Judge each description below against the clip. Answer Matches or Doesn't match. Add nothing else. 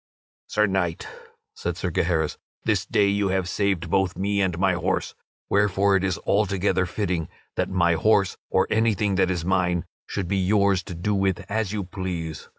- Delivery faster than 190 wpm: Doesn't match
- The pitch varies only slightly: Matches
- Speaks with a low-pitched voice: Matches